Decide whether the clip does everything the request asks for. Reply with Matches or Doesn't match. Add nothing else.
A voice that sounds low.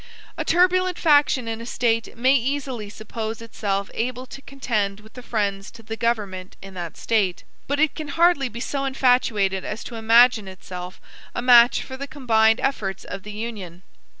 Doesn't match